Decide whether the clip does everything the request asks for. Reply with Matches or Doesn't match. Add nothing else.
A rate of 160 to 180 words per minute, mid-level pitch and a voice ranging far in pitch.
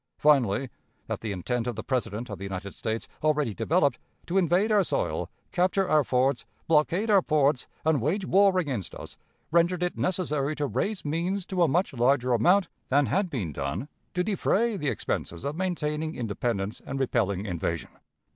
Matches